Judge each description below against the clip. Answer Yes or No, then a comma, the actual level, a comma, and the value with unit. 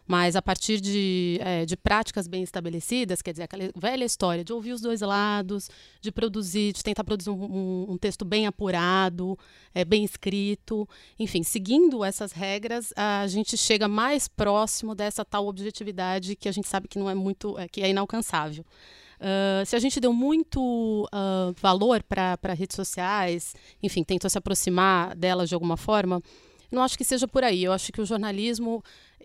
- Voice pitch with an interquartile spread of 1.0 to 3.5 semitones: Yes, narrow, 2.6 semitones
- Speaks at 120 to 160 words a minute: No, average, 170 wpm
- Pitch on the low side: No, high, 200 Hz